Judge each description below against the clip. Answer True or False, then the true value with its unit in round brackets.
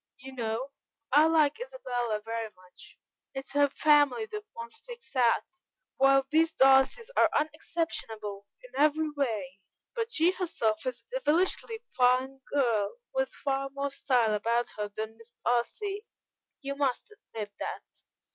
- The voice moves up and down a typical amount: False (5.9 semitones)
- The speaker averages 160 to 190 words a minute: False (145 wpm)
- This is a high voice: True (270 Hz)